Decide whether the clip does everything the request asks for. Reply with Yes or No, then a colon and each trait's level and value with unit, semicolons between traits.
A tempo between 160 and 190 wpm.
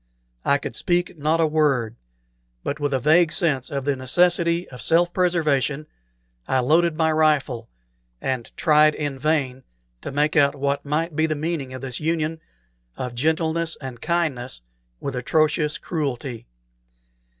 No: average, 150 wpm